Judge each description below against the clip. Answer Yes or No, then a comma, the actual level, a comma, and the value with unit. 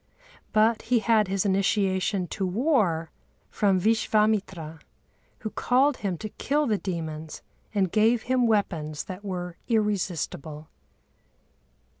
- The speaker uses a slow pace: Yes, slow, 115 wpm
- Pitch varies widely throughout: No, average, 3.7 semitones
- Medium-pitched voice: No, high, 200 Hz